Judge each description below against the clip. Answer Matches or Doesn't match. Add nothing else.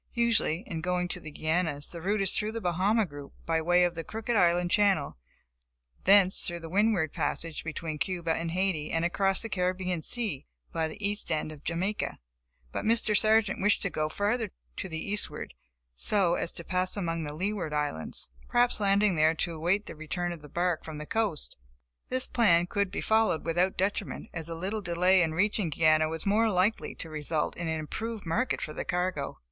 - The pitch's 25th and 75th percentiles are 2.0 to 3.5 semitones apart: Doesn't match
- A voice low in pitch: Doesn't match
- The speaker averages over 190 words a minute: Matches